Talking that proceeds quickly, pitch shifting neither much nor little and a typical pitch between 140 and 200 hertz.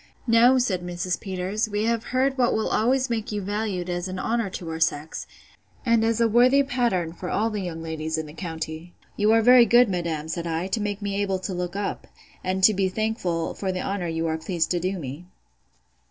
Yes: fast, 220 wpm; average, 4.4 semitones; high, 190 Hz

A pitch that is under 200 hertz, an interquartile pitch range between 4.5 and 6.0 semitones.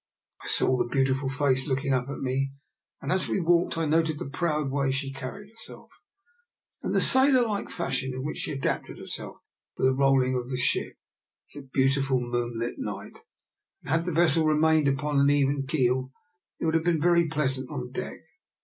No: medium, 140 Hz; average, 3.3 semitones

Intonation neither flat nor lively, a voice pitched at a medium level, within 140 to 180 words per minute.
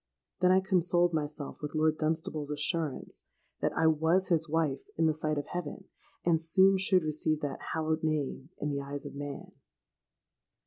No: narrow, 2.3 semitones; medium, 155 Hz; average, 170 wpm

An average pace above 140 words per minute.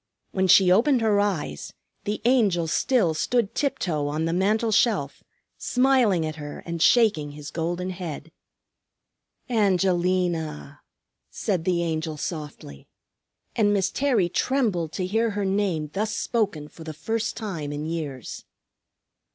No: slow, 135 wpm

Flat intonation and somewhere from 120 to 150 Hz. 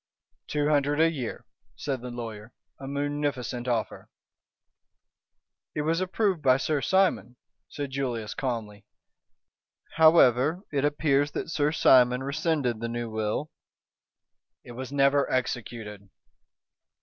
No: average, 3.7 semitones; low, 135 Hz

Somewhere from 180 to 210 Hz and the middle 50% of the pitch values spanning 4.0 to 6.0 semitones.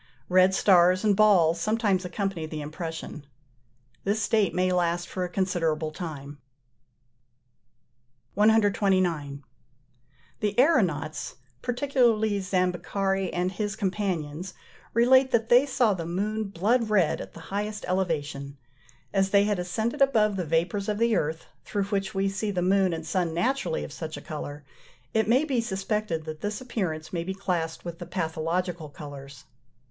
Yes: medium, 185 Hz; average, 4.3 semitones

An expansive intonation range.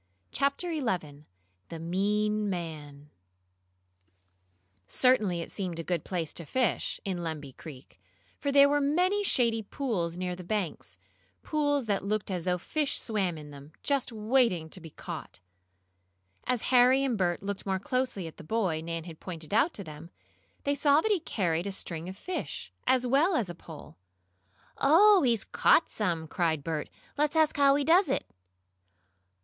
Yes: wide, 8.4 semitones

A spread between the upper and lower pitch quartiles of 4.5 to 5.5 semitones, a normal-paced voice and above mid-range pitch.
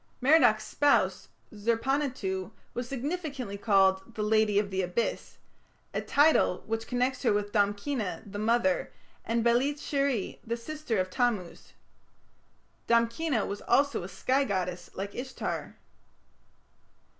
No: average, 4.9 semitones; slow, 125 wpm; high, 230 Hz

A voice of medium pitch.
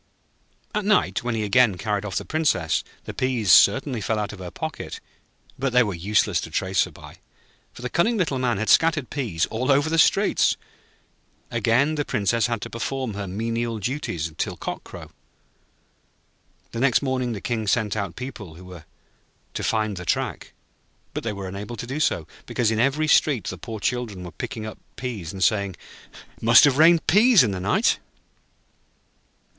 No: low, 115 Hz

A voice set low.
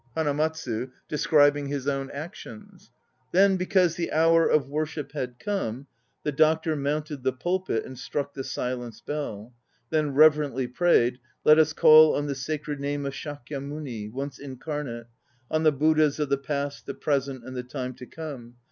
No: medium, 145 Hz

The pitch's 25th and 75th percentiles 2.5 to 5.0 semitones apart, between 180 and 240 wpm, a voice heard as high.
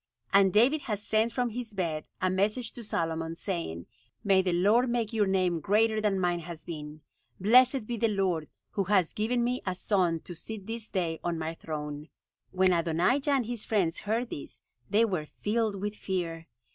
Yes: average, 4.6 semitones; average, 185 wpm; high, 195 Hz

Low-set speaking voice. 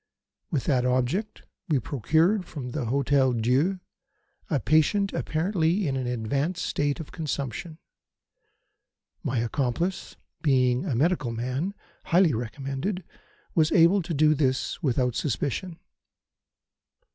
No: medium, 145 Hz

